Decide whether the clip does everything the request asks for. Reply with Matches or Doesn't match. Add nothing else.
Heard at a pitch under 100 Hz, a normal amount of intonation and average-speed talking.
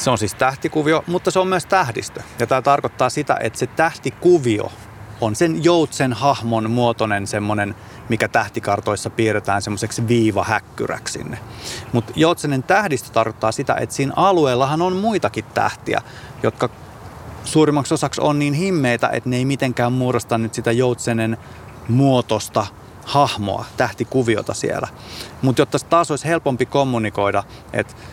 Doesn't match